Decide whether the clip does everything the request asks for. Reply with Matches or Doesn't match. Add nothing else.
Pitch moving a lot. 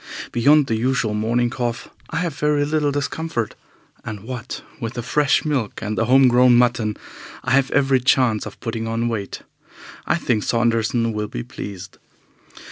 Doesn't match